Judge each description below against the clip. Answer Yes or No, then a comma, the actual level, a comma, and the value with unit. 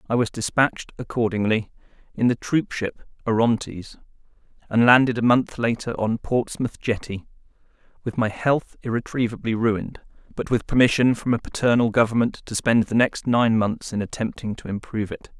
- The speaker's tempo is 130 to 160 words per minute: Yes, average, 150 wpm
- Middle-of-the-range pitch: No, low, 115 Hz